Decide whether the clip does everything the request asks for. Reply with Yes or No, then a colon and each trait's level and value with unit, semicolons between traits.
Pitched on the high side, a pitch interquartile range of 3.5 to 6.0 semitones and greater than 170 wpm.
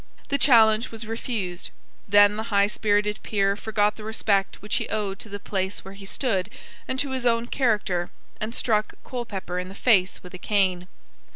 No: high, 210 Hz; narrow, 2.6 semitones; average, 185 wpm